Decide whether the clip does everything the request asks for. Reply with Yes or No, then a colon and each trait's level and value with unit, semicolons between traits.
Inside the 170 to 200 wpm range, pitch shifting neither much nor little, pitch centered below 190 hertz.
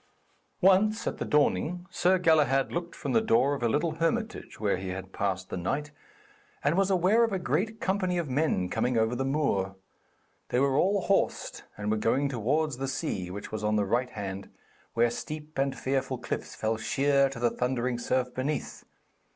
No: average, 190 wpm; wide, 6.9 semitones; low, 135 Hz